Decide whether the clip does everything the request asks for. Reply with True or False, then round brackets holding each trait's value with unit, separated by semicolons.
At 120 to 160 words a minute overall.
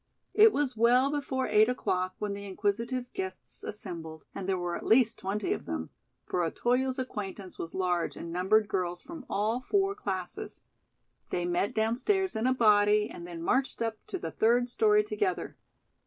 False (170 wpm)